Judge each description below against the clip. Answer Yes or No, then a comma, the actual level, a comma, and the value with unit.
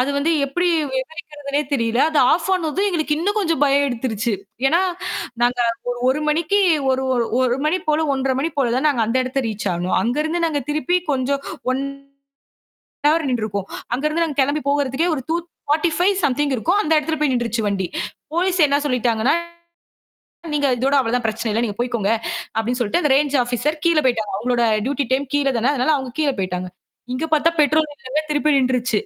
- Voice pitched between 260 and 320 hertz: Yes, very high, 280 Hz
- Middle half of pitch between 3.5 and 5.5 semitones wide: Yes, average, 4.0 semitones